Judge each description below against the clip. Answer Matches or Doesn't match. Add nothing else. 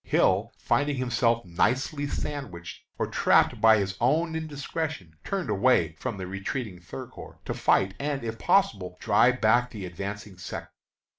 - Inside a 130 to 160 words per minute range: Matches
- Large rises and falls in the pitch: Matches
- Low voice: Matches